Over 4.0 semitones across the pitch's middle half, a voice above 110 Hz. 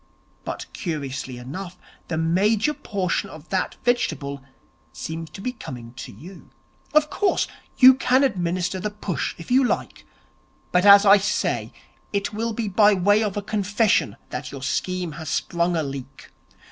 Yes: average, 4.7 semitones; high, 190 Hz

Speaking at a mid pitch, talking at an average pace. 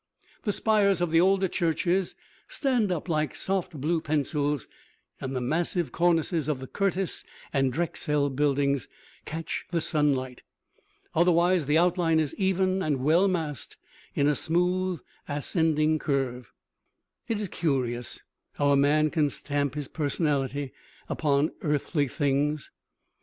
No: medium, 155 Hz; slow, 130 wpm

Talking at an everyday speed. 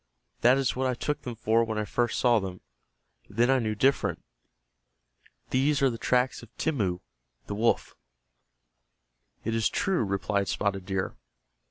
Yes: average, 155 wpm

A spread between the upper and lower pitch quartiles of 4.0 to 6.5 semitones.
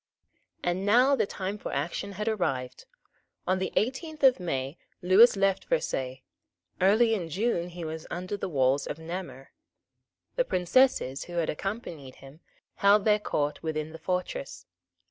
Yes: average, 5.1 semitones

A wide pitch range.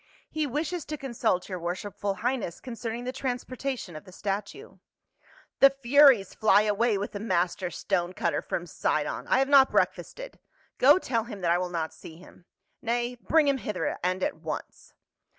Yes: wide, 6.5 semitones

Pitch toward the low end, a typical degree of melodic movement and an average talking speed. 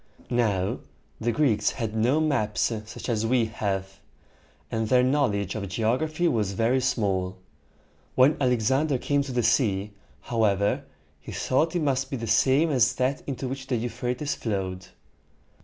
Yes: low, 120 Hz; average, 3.9 semitones; average, 150 wpm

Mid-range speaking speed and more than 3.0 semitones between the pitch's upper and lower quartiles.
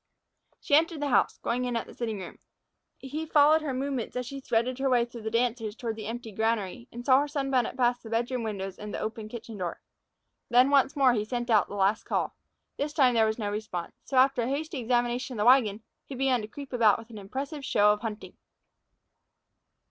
No: fast, 220 wpm; average, 3.4 semitones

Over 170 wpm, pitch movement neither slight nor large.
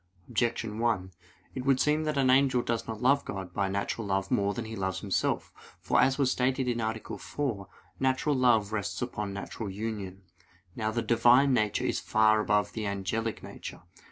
Yes: average, 180 wpm; average, 3.9 semitones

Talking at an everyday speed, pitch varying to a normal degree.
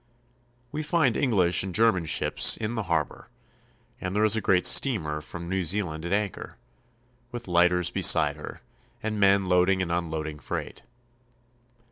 Yes: average, 150 wpm; average, 3.8 semitones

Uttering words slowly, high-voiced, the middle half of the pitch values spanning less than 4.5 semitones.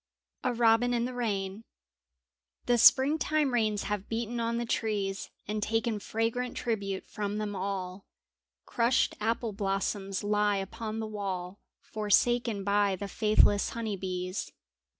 Yes: slow, 130 wpm; high, 210 Hz; average, 2.8 semitones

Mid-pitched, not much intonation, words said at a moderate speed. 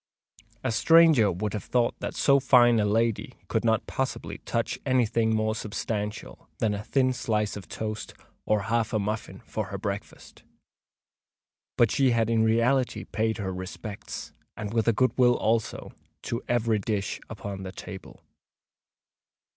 No: low, 110 Hz; narrow, 2.3 semitones; average, 150 wpm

